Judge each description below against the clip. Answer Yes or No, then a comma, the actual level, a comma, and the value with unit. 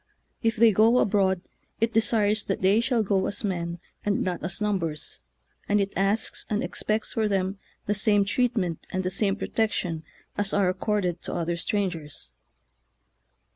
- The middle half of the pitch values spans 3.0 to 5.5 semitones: No, narrow, 2.6 semitones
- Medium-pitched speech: No, high, 200 Hz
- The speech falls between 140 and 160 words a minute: No, average, 170 wpm